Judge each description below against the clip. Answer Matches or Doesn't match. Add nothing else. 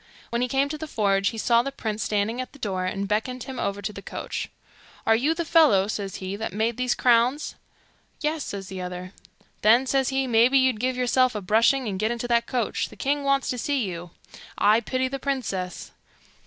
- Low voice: Doesn't match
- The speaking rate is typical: Doesn't match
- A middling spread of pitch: Matches